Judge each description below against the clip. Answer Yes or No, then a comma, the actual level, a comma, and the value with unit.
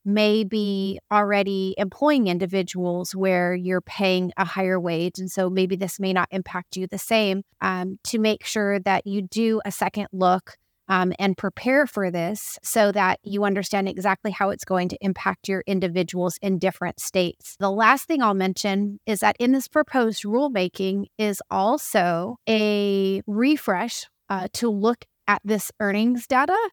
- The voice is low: No, high, 195 Hz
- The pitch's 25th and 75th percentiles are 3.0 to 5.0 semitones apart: No, narrow, 2.4 semitones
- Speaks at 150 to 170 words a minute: Yes, average, 165 wpm